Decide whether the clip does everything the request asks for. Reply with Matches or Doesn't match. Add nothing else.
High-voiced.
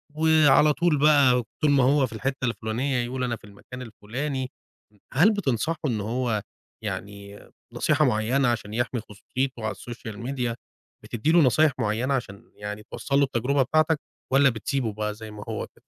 Doesn't match